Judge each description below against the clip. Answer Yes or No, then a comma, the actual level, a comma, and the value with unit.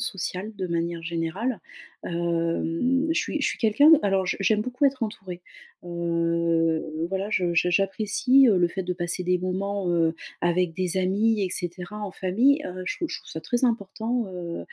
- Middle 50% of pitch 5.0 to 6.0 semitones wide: No, average, 3.8 semitones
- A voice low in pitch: No, medium, 185 Hz